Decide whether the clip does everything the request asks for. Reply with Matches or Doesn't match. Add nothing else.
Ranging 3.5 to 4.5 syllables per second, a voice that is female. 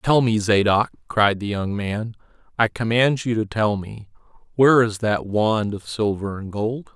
Doesn't match